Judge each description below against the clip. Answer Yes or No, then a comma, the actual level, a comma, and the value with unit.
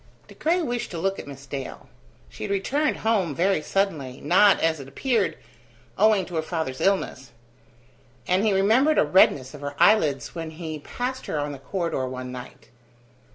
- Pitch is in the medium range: Yes, medium, 165 Hz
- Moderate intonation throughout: No, wide, 6.3 semitones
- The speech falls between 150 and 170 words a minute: No, average, 180 wpm